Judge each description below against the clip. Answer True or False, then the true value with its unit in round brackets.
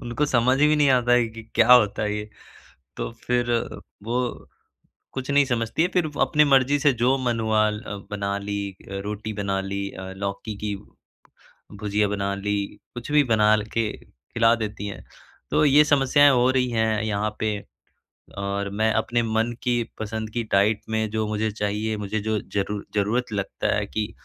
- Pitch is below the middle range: True (110 Hz)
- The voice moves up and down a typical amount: True (3.1 semitones)